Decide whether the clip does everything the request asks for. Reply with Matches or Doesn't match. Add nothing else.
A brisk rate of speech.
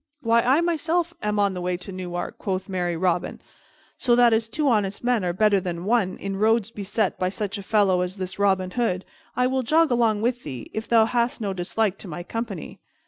Matches